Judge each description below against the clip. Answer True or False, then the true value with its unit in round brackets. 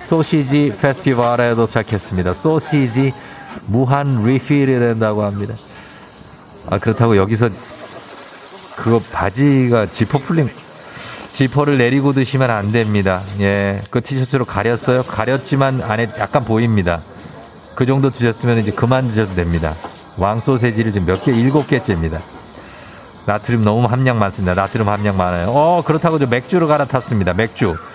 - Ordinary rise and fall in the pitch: True (4.9 semitones)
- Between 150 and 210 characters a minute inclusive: False (315 characters per minute)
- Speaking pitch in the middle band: False (115 Hz)